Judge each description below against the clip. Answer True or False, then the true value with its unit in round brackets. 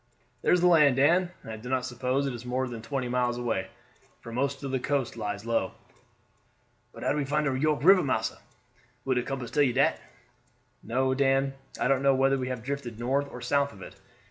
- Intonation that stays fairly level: True (2.3 semitones)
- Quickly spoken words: True (220 wpm)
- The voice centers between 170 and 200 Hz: False (130 Hz)